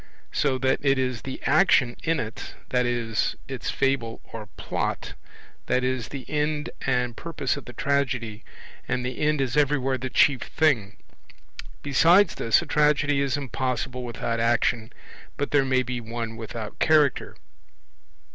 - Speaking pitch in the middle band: No, low, 130 Hz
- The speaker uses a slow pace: No, average, 145 wpm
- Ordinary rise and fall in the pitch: Yes, average, 3.1 semitones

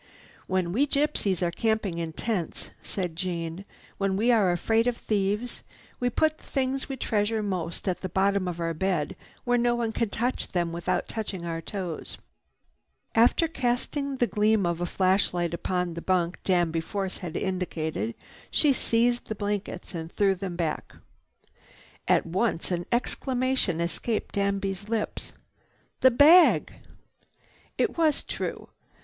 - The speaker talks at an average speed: Yes, average, 150 wpm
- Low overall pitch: No, high, 195 Hz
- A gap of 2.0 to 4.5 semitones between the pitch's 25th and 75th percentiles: No, average, 5.2 semitones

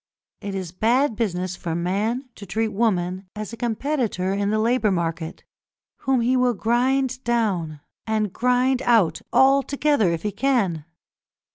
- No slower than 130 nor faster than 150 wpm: Yes, average, 145 wpm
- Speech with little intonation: No, average, 5.2 semitones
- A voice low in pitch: No, high, 220 Hz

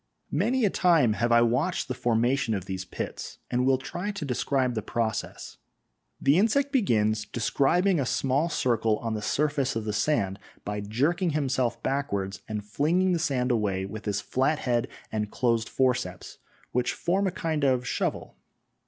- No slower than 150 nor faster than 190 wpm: Yes, average, 170 wpm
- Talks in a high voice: No, low, 125 Hz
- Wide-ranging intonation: Yes, wide, 5.7 semitones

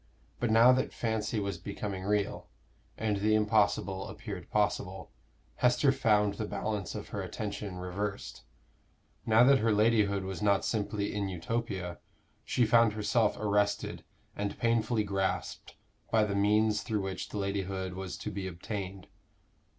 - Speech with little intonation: Yes, narrow, 2.0 semitones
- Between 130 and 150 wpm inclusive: Yes, average, 145 wpm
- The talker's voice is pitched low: Yes, low, 105 Hz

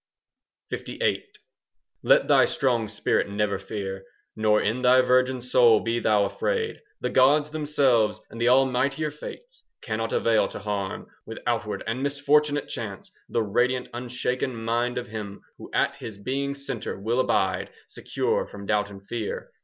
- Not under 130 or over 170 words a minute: Yes, average, 155 wpm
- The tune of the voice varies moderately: Yes, average, 3.9 semitones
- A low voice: Yes, low, 120 Hz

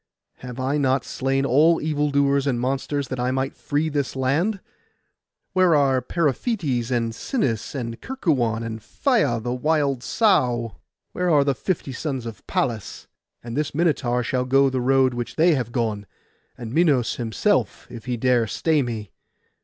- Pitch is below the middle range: Yes, low, 130 Hz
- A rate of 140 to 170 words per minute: Yes, average, 160 wpm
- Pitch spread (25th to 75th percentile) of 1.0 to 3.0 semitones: No, average, 3.6 semitones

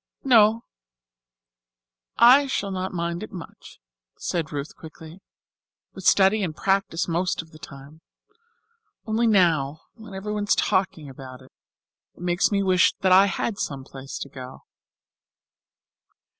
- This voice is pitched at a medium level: Yes, medium, 180 Hz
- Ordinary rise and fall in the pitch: Yes, average, 4.5 semitones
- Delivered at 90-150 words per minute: Yes, slow, 135 wpm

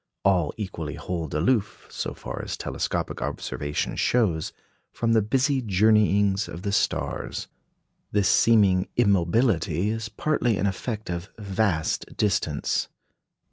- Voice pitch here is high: No, low, 100 Hz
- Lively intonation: No, average, 3.8 semitones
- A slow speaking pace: Yes, slow, 120 wpm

